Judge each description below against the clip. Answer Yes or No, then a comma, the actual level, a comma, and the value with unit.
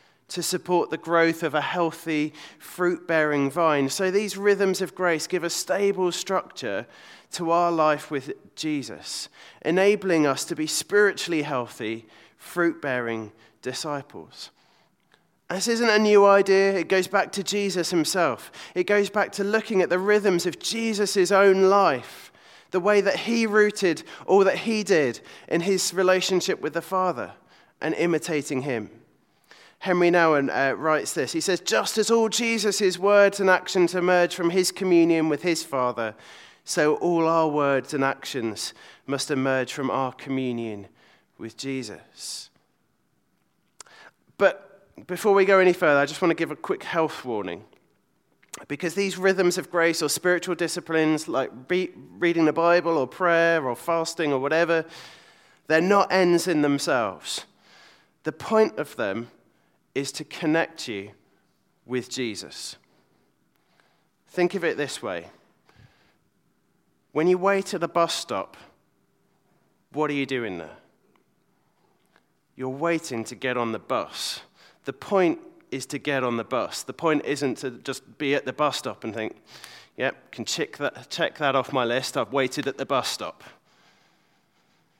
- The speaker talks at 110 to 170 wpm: Yes, average, 155 wpm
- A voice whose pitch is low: No, medium, 170 Hz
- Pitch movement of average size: Yes, average, 4.9 semitones